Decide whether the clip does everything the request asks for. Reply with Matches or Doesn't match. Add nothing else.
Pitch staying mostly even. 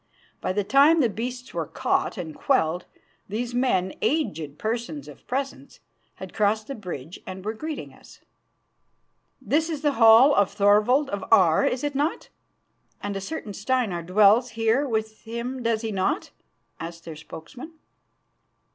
Doesn't match